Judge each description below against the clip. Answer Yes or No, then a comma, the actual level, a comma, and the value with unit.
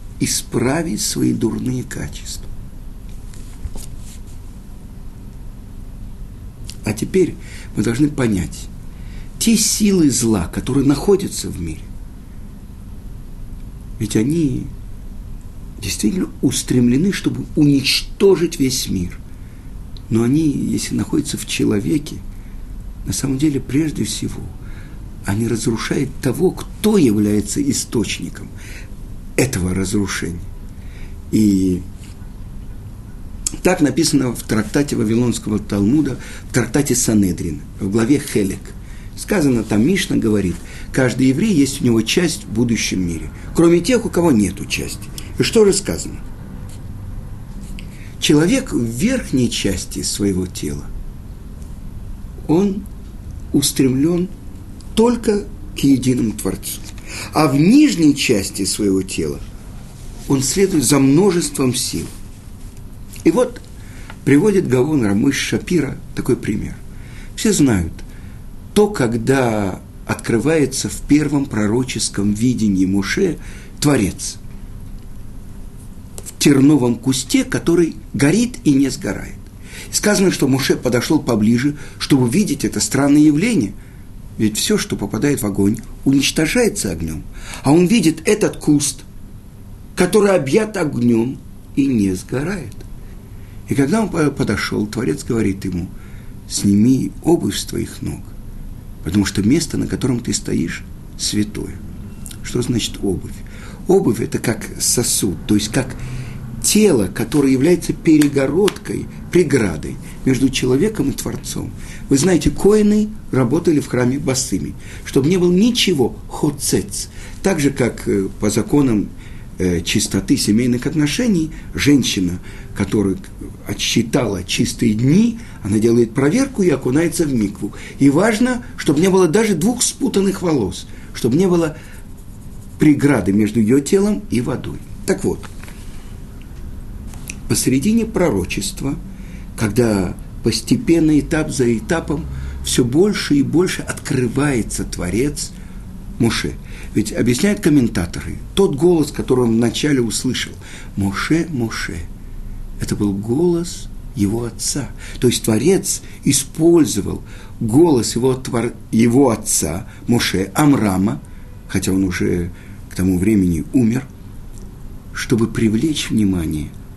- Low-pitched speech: Yes, low, 110 Hz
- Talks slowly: Yes, slow, 105 wpm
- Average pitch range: No, wide, 6.2 semitones